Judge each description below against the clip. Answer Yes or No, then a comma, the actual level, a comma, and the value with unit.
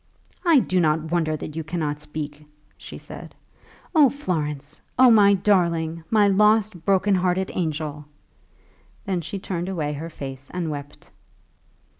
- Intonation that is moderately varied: Yes, average, 4.4 semitones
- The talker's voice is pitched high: No, medium, 170 Hz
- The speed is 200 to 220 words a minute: No, average, 140 wpm